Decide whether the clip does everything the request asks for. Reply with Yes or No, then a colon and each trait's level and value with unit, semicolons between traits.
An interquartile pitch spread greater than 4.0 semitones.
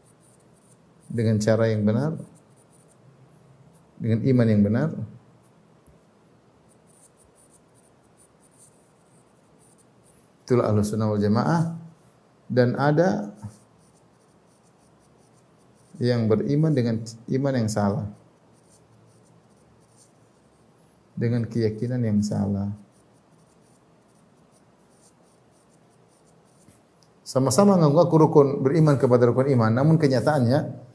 Yes: wide, 5.5 semitones